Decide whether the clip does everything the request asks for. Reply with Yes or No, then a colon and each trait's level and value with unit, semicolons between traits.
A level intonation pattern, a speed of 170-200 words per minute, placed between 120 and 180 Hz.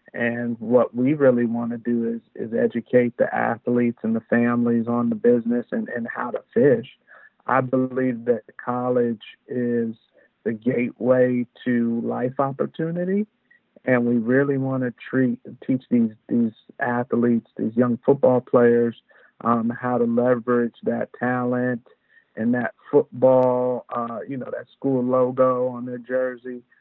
No: narrow, 1.4 semitones; average, 145 wpm; low, 125 Hz